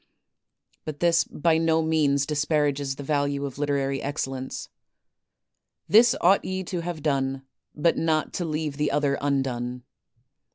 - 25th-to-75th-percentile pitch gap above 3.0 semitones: No, narrow, 2.6 semitones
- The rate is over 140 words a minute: No, slow, 135 wpm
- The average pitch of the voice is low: No, medium, 145 Hz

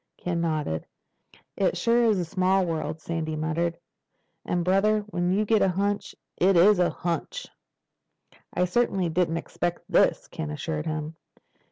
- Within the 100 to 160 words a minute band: Yes, average, 150 wpm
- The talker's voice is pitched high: No, medium, 175 Hz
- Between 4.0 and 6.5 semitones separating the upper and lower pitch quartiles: No, average, 3.1 semitones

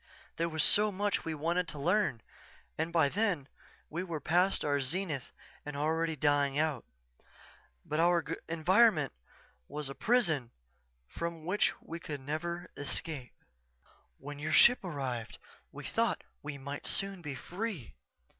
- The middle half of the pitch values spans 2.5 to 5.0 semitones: Yes, average, 3.7 semitones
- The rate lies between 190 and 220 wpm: No, average, 140 wpm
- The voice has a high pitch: No, medium, 160 Hz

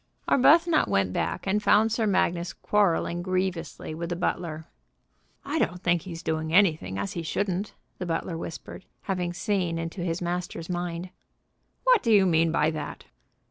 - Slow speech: No, average, 160 wpm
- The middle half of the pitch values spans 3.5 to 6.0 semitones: No, average, 2.7 semitones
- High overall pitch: No, medium, 175 Hz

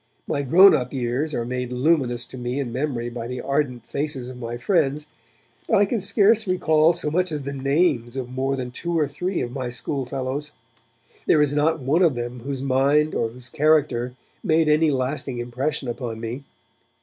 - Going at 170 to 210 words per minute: Yes, average, 190 wpm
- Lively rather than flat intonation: No, average, 3.6 semitones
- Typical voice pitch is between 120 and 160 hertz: Yes, low, 135 Hz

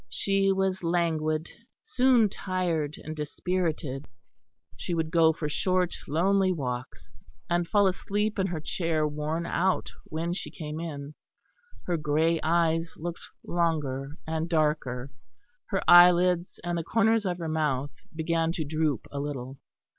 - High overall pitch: No, medium, 165 Hz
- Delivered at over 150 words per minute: No, average, 140 wpm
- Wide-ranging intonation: No, average, 2.9 semitones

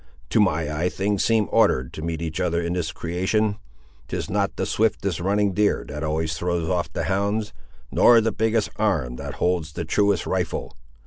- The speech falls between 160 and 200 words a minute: Yes, average, 185 wpm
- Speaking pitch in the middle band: No, very low, 90 Hz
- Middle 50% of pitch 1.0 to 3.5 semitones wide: No, average, 4.2 semitones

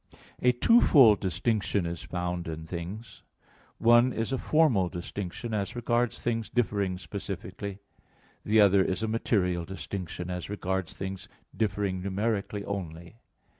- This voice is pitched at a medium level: No, low, 100 Hz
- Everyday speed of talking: No, slow, 130 wpm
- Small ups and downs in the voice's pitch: No, average, 3.8 semitones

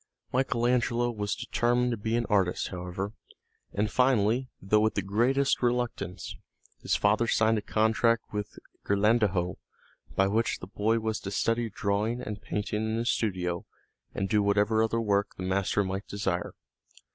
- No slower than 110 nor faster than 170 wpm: Yes, average, 160 wpm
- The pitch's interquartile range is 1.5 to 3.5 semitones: Yes, narrow, 2.6 semitones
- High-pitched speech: No, low, 105 Hz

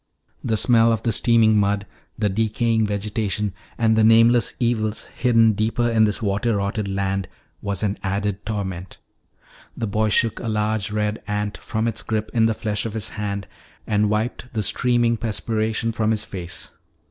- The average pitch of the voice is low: Yes, low, 110 Hz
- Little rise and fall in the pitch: Yes, narrow, 1.7 semitones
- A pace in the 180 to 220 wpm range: No, average, 170 wpm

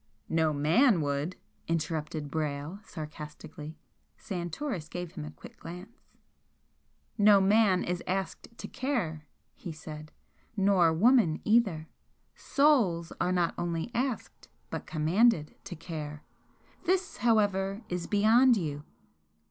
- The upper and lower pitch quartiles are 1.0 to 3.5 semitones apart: No, wide, 5.4 semitones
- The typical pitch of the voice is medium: Yes, medium, 175 Hz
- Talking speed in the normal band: No, slow, 115 wpm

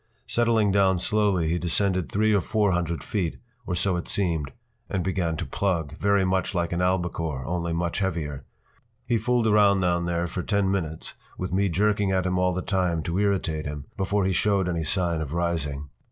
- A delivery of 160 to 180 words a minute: No, average, 195 wpm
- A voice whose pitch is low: Yes, very low, 90 Hz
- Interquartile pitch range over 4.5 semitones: No, average, 2.8 semitones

